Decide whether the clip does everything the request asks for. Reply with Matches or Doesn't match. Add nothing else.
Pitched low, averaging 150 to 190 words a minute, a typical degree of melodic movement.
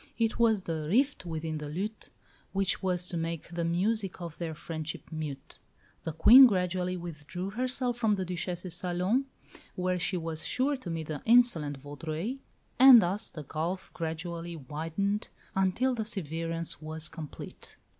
Doesn't match